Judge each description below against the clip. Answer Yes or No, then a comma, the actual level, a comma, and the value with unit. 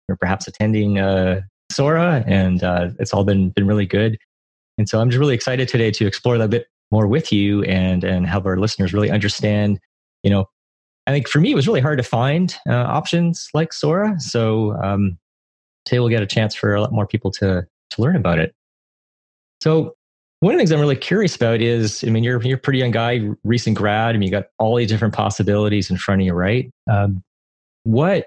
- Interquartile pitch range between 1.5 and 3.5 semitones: No, average, 4.1 semitones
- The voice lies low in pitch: Yes, low, 105 Hz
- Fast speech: Yes, fast, 220 wpm